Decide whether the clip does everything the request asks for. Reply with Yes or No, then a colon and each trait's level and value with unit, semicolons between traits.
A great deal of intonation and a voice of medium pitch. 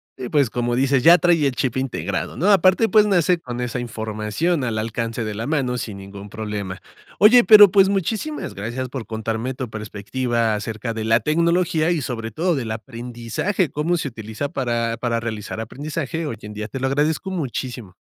No: wide, 6.2 semitones; low, 125 Hz